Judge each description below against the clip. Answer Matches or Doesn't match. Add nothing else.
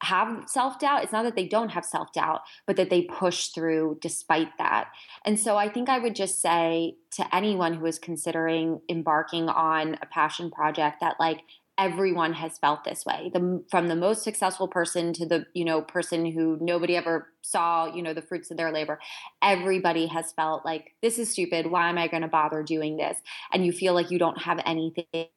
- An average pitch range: Doesn't match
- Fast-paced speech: Matches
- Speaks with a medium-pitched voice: Matches